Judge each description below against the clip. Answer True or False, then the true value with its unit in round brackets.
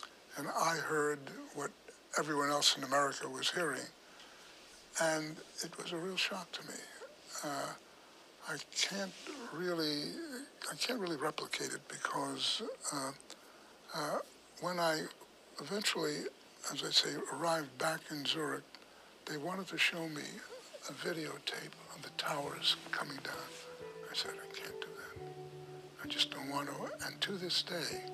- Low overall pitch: False (165 Hz)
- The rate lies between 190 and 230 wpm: False (145 wpm)